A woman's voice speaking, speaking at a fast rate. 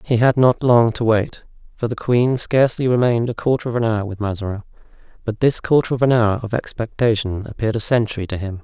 No: male; fast, 215 wpm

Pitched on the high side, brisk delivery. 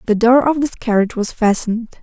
Yes: high, 230 Hz; fast, 210 wpm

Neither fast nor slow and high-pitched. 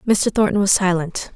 Yes: average, 180 wpm; high, 195 Hz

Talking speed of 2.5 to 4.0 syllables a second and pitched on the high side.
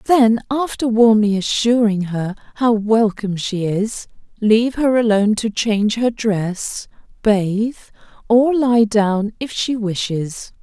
Yes: 3.9 syllables/s; high, 220 Hz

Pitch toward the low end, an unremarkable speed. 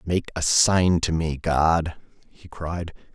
Yes: very low, 80 Hz; average, 155 wpm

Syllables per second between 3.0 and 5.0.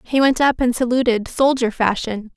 Yes: 4.9 syllables/s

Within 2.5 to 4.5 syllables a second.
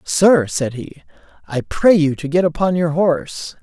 Yes: 4.4 syllables/s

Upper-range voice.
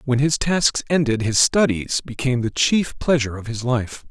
No: low, 130 Hz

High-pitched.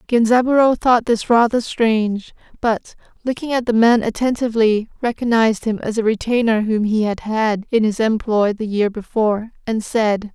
Yes: high, 225 Hz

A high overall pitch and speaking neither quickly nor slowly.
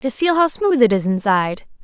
No: high, 245 Hz; fast, 230 wpm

